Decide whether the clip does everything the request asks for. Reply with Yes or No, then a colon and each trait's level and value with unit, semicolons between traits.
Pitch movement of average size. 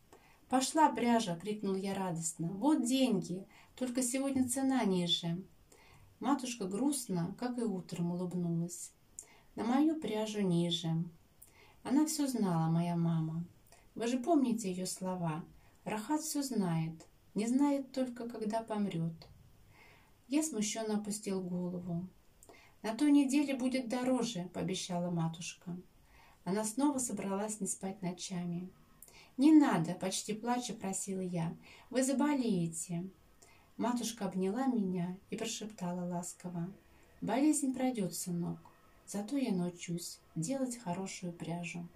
No: wide, 6.2 semitones